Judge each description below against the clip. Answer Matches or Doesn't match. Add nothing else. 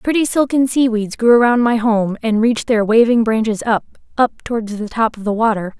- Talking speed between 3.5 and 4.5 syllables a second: Doesn't match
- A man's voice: Doesn't match